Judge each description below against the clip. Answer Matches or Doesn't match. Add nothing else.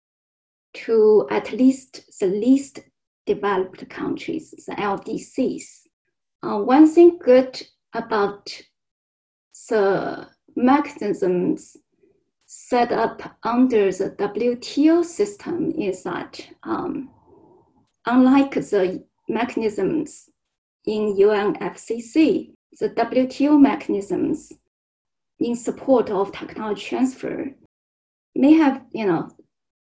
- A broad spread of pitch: Matches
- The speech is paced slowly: Matches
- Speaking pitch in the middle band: Doesn't match